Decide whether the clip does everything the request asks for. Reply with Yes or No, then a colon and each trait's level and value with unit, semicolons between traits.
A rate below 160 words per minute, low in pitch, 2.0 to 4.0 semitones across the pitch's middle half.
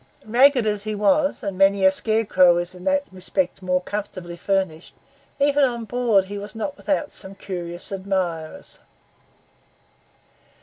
No: average, 140 wpm; high, 195 Hz; average, 3.7 semitones